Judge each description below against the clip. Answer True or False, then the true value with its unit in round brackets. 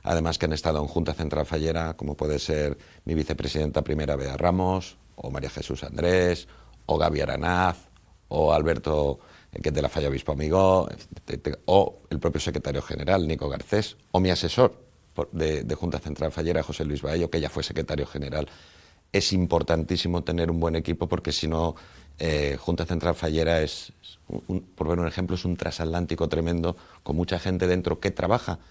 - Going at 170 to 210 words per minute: True (180 wpm)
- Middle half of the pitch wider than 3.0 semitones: False (2.7 semitones)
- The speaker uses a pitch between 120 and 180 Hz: False (80 Hz)